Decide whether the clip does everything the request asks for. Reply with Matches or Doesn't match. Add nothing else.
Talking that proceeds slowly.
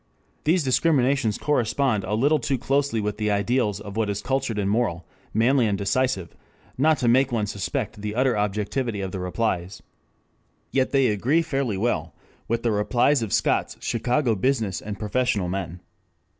Doesn't match